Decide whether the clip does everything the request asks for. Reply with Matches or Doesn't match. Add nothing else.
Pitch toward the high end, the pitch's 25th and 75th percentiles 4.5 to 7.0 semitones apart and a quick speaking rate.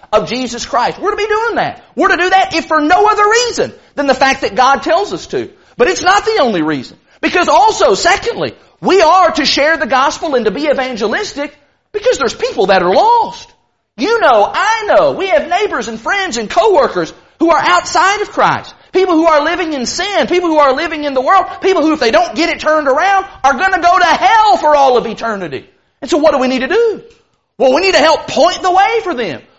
Matches